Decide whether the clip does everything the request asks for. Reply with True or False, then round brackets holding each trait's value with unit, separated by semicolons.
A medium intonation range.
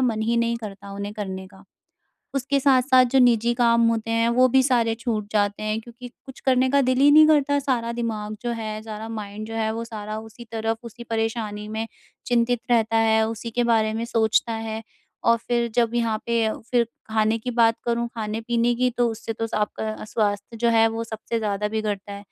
False (1.7 semitones)